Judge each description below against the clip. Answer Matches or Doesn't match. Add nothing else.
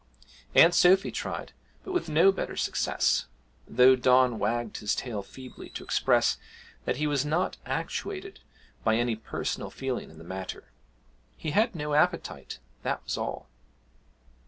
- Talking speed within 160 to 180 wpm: Doesn't match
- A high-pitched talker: Doesn't match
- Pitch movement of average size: Doesn't match